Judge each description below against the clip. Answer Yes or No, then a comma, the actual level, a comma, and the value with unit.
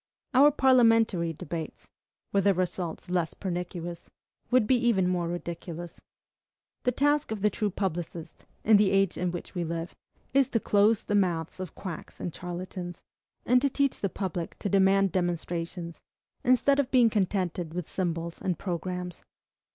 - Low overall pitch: No, medium, 185 Hz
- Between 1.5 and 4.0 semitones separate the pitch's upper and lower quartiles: Yes, average, 3.6 semitones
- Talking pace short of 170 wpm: Yes, average, 155 wpm